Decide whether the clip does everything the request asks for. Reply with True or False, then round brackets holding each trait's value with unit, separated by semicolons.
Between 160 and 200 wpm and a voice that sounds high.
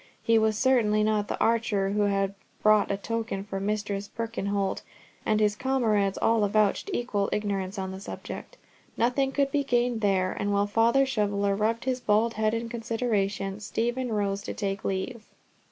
True (170 wpm; 215 Hz)